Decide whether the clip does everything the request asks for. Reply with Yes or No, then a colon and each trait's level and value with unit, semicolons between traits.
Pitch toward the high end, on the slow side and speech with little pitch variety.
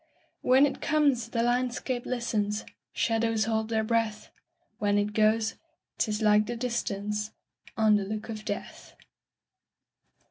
Yes: high, 220 Hz; slow, 115 wpm; narrow, 2.2 semitones